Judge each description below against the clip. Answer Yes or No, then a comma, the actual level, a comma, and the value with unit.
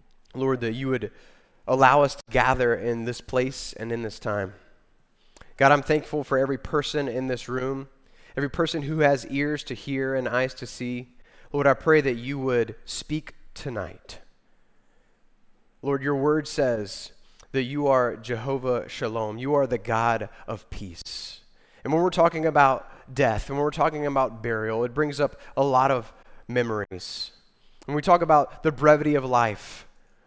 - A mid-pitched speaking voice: No, low, 130 Hz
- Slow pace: No, average, 170 wpm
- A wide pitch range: No, average, 3.4 semitones